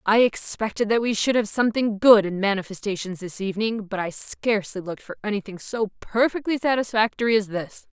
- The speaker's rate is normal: Yes, average, 175 wpm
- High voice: Yes, high, 210 Hz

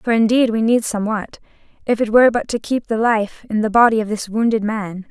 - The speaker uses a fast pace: Yes, fast, 235 wpm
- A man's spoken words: No, female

